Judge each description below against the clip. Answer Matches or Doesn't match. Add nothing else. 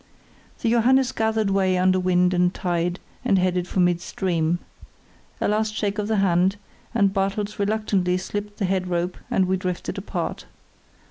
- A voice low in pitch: Doesn't match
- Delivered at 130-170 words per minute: Matches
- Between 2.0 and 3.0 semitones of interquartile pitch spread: Matches